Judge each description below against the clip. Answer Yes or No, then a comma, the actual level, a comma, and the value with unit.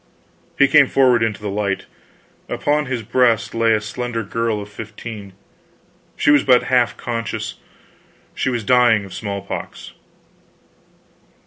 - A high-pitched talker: No, low, 115 Hz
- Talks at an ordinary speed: No, slow, 130 wpm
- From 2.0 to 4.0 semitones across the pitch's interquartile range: Yes, average, 3.1 semitones